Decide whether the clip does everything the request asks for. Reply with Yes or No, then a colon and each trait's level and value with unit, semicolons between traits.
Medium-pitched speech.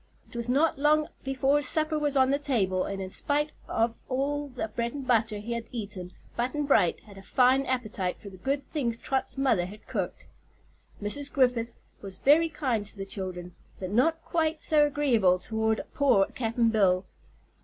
No: high, 245 Hz